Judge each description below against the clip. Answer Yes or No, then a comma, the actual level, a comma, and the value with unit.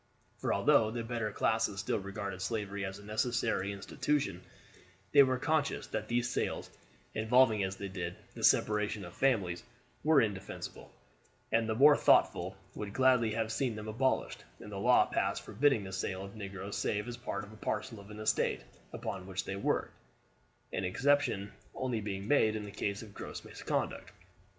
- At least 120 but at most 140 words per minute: No, average, 170 wpm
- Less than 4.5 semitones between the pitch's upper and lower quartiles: Yes, average, 3.4 semitones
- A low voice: Yes, low, 110 Hz